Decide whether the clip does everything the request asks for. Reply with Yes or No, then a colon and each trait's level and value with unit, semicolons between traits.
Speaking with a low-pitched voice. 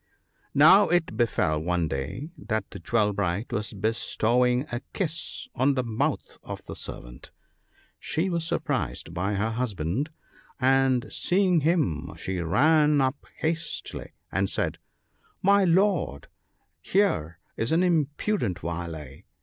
Yes: low, 125 Hz